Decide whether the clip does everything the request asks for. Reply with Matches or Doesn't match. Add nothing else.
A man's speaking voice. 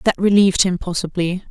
Doesn't match